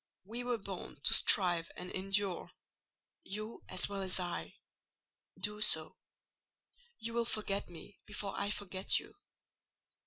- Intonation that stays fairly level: Yes, narrow, 2.3 semitones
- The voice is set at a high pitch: Yes, high, 200 Hz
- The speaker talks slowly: Yes, slow, 125 wpm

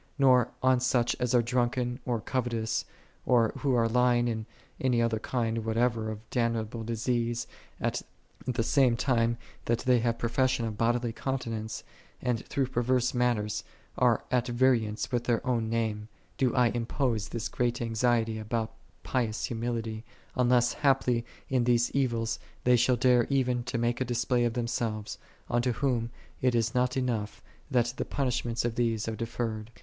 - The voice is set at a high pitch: No, low, 120 Hz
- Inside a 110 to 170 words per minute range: Yes, average, 160 wpm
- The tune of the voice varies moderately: No, narrow, 1.6 semitones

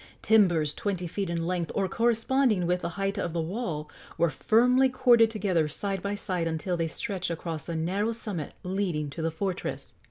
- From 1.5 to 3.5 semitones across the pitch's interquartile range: No, average, 4.2 semitones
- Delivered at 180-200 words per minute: Yes, average, 185 wpm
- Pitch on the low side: No, medium, 185 Hz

